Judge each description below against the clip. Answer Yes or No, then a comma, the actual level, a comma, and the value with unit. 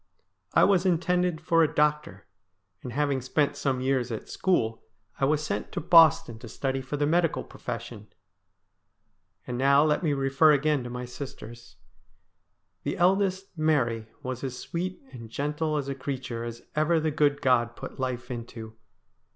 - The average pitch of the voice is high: No, medium, 140 Hz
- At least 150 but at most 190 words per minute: Yes, average, 160 wpm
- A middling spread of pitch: Yes, average, 4.1 semitones